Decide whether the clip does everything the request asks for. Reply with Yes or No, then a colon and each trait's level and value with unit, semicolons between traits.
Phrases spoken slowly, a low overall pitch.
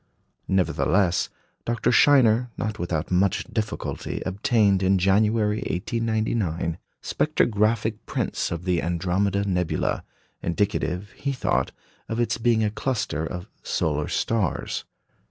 Yes: slow, 110 wpm; low, 100 Hz